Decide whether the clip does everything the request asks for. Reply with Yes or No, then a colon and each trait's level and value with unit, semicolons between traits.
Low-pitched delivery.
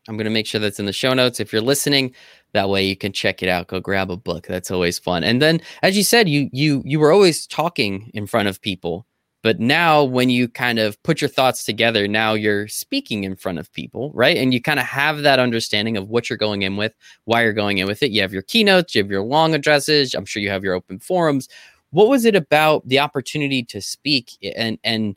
Yes: low, 115 Hz